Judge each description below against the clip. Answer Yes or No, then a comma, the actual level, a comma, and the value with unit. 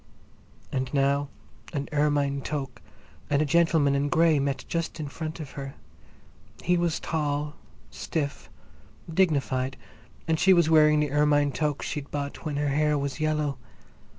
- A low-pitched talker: No, medium, 145 Hz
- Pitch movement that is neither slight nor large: No, narrow, 1.8 semitones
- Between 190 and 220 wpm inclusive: No, average, 150 wpm